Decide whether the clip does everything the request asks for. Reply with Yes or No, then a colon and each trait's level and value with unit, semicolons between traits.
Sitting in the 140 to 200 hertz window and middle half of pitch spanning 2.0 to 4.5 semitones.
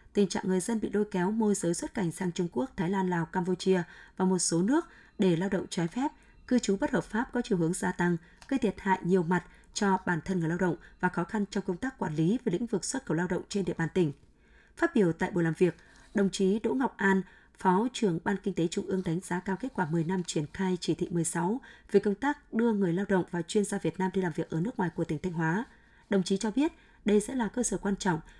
Yes: high, 190 Hz; average, 3.5 semitones